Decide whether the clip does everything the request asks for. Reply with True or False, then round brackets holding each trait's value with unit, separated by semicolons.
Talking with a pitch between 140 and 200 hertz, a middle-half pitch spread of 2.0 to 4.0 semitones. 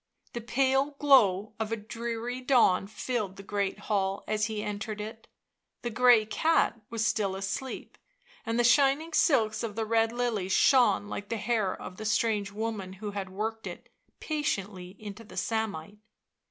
False (220 Hz; 2.8 semitones)